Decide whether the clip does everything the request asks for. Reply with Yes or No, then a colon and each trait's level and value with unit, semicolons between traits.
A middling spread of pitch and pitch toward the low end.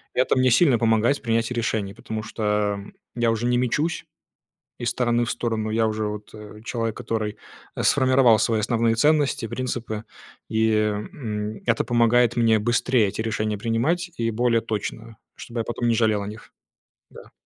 No: narrow, 1.9 semitones; low, 115 Hz